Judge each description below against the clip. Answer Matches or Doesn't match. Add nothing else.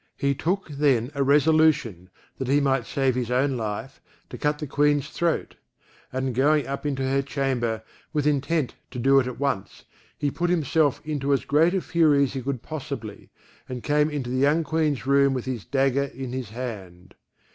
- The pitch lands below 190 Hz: Matches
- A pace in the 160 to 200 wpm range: Matches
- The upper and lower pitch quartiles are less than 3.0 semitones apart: Matches